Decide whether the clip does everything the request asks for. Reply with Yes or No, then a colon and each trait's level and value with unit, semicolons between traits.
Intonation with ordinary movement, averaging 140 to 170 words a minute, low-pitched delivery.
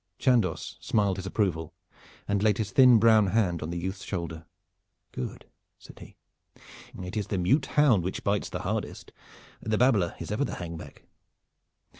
Yes: average, 4.0 semitones; average, 165 wpm; low, 100 Hz